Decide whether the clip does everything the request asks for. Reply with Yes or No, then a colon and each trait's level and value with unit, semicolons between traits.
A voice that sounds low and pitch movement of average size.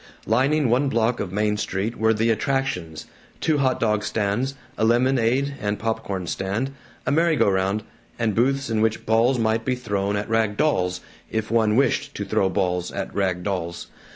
Yes: low, 110 Hz; average, 4.1 semitones